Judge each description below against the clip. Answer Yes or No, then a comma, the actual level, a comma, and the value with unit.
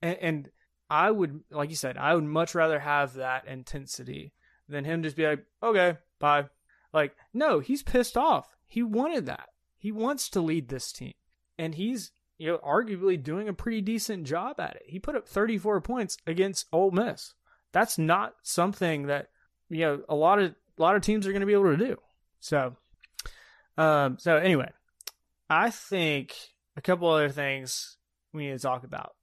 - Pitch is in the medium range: Yes, medium, 170 Hz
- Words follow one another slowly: No, average, 185 wpm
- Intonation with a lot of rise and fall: Yes, wide, 5.7 semitones